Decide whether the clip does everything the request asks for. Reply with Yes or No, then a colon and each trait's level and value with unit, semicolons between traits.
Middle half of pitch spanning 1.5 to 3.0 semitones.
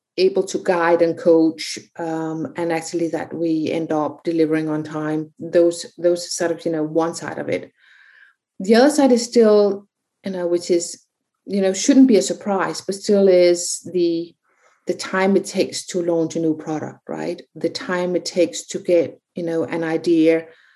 Yes: narrow, 2.5 semitones